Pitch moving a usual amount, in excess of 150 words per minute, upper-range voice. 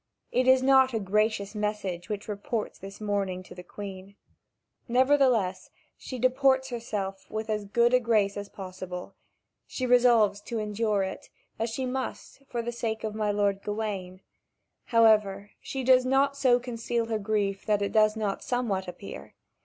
Yes: average, 3.5 semitones; average, 160 wpm; high, 215 Hz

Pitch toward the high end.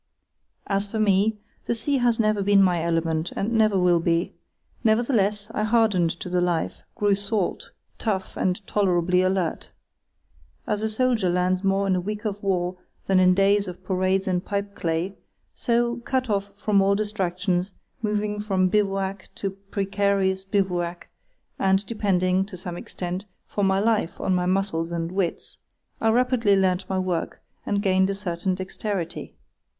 Yes: high, 195 Hz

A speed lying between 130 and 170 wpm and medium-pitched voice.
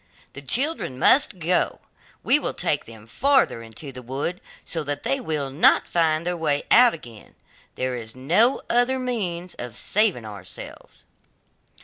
Yes: average, 150 wpm; medium, 160 Hz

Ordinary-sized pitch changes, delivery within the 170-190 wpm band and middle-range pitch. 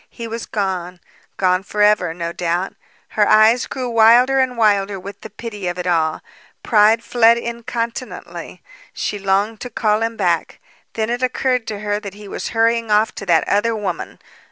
No: average, 3.0 semitones; average, 175 wpm; high, 210 Hz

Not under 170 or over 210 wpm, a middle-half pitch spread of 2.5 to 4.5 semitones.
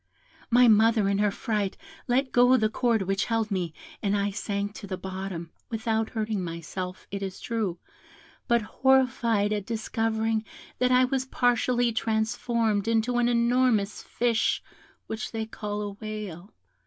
No: average, 150 wpm; average, 2.9 semitones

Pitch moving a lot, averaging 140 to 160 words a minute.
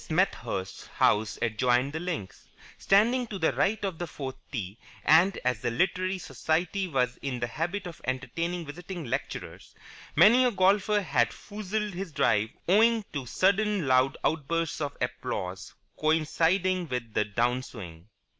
Yes: wide, 7.2 semitones; average, 145 wpm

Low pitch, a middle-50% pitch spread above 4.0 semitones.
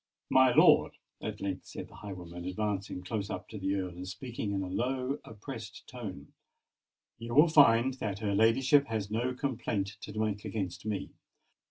Yes: low, 110 Hz; average, 4.4 semitones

